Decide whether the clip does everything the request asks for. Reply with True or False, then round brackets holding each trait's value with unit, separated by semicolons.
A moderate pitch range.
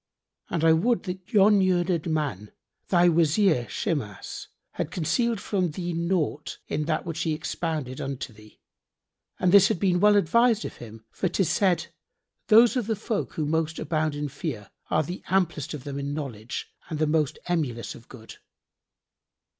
True (4.3 semitones)